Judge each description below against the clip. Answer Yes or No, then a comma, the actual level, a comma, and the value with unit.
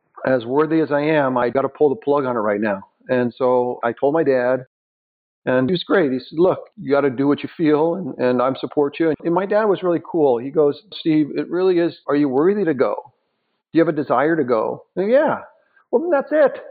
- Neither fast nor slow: No, fast, 255 wpm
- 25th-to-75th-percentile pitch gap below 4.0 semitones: No, average, 4.7 semitones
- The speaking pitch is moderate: Yes, medium, 145 Hz